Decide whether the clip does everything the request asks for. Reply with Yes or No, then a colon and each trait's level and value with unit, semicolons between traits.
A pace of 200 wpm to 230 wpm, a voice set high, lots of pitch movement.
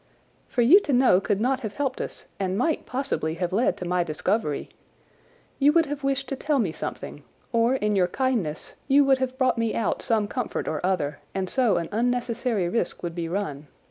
Yes: fast, 205 wpm; high, 230 Hz; wide, 6.4 semitones